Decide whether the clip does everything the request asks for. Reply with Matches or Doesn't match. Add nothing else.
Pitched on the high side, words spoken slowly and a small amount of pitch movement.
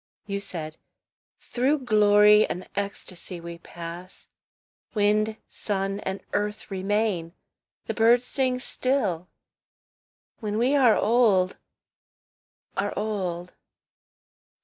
Doesn't match